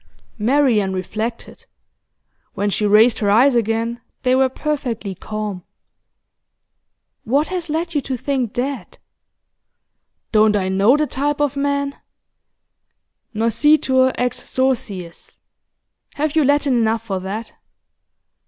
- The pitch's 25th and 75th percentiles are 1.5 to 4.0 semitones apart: No, average, 4.9 semitones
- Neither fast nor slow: No, slow, 115 wpm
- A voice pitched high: Yes, high, 245 Hz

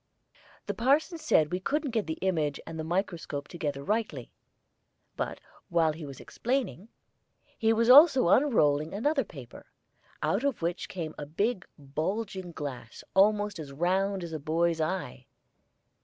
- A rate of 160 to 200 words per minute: No, average, 145 wpm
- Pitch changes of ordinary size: No, wide, 6.2 semitones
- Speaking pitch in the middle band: Yes, medium, 180 Hz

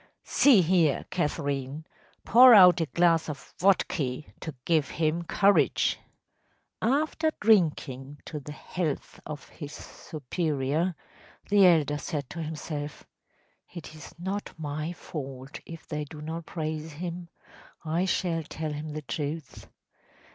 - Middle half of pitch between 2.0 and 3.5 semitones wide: Yes, average, 3.0 semitones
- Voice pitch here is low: No, medium, 160 Hz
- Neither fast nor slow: No, slow, 125 wpm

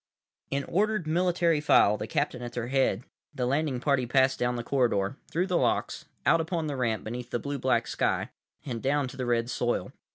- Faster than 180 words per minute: Yes, fast, 205 wpm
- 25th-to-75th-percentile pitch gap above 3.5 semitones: Yes, average, 3.9 semitones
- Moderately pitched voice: No, low, 130 Hz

